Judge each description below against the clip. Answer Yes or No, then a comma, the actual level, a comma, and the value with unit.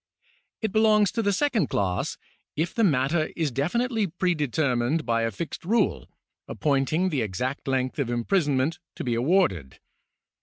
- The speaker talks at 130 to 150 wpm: Yes, average, 145 wpm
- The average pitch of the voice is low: No, medium, 150 Hz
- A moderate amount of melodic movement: No, wide, 6.8 semitones